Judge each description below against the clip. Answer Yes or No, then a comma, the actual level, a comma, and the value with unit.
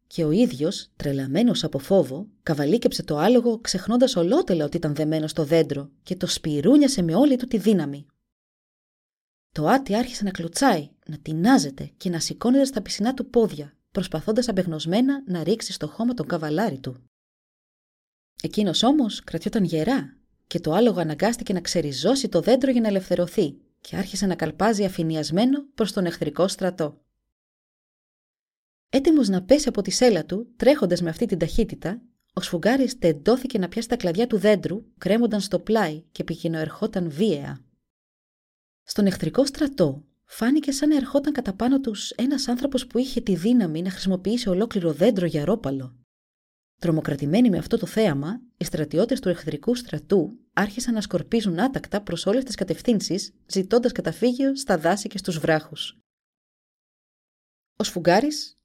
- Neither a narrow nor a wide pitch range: No, wide, 6.5 semitones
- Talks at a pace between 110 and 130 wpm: No, average, 150 wpm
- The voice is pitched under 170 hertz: No, high, 195 Hz